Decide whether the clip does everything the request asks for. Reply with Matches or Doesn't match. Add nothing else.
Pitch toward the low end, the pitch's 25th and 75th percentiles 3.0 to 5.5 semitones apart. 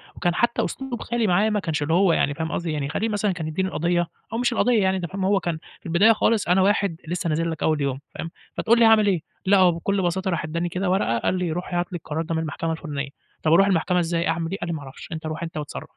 Doesn't match